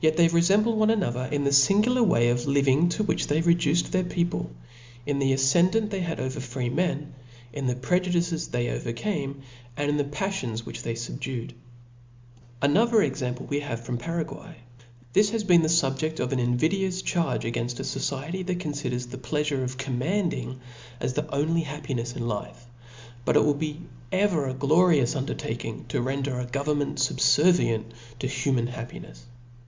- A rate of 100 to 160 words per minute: No, average, 170 wpm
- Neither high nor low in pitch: Yes, medium, 145 Hz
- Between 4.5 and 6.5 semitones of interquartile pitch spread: Yes, average, 5.3 semitones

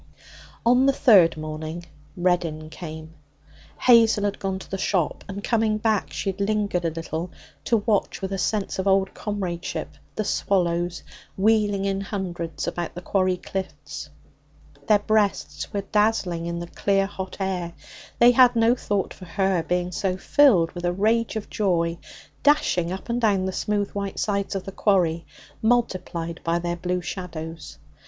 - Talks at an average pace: Yes, average, 160 wpm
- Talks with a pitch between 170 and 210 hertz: Yes, high, 190 Hz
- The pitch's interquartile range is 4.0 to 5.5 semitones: No, average, 3.2 semitones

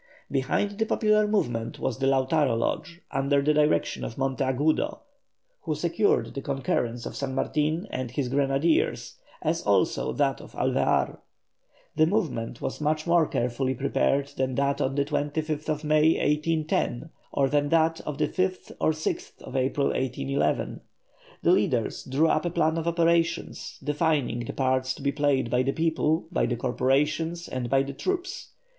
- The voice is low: No, medium, 145 Hz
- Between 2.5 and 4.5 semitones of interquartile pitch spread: Yes, average, 3.4 semitones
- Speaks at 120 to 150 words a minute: No, average, 160 wpm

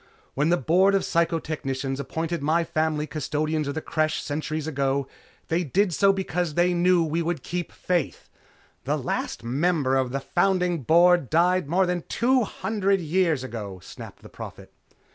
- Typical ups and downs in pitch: Yes, average, 3.5 semitones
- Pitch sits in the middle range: Yes, medium, 165 Hz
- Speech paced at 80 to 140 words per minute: No, average, 165 wpm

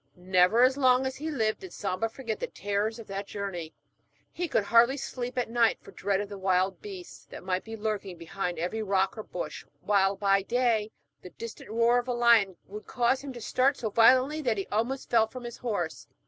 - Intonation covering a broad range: No, average, 3.8 semitones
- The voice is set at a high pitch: Yes, high, 220 Hz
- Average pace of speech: No, fast, 215 wpm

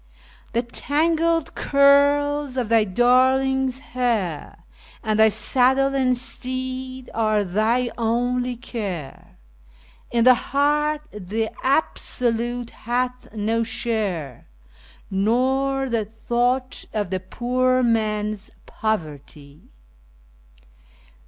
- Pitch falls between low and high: No, high, 240 Hz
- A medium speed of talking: No, slow, 85 wpm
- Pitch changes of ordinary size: Yes, average, 3.4 semitones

